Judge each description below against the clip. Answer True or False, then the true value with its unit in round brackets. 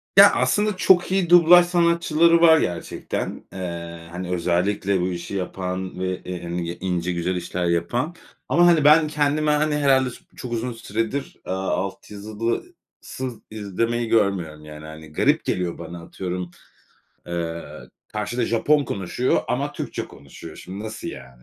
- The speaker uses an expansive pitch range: True (8.8 semitones)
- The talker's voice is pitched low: True (100 Hz)